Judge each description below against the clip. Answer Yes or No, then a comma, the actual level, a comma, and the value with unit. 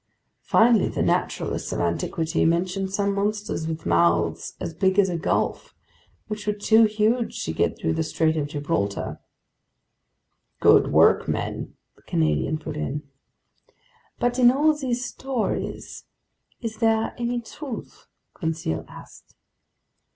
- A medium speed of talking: No, slow, 130 wpm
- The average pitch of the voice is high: Yes, high, 195 Hz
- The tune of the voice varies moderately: No, wide, 6.3 semitones